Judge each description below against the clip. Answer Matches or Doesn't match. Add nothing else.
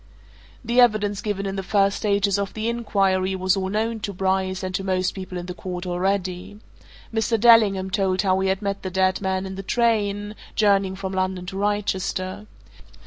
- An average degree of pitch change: Doesn't match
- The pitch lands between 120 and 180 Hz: Doesn't match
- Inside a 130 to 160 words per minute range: Doesn't match